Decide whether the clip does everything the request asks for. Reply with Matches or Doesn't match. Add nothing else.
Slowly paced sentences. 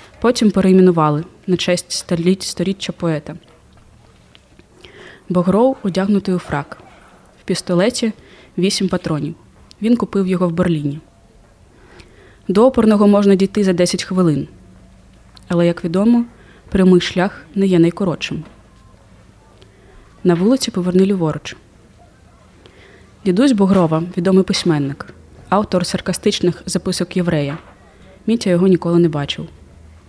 Matches